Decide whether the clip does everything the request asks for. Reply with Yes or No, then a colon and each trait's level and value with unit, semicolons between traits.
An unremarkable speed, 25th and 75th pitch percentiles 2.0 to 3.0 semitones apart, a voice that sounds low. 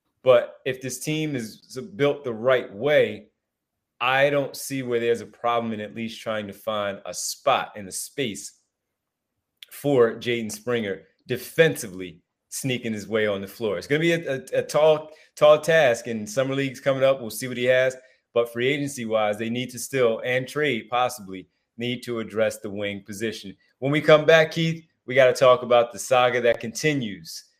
No: average, 190 wpm; average, 3.4 semitones; low, 125 Hz